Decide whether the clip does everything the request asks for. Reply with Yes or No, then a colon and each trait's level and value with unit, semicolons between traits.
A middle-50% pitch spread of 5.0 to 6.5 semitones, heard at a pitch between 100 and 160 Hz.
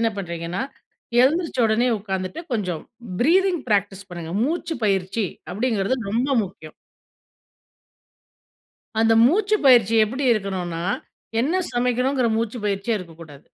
No: wide, 5.5 semitones; high, 220 Hz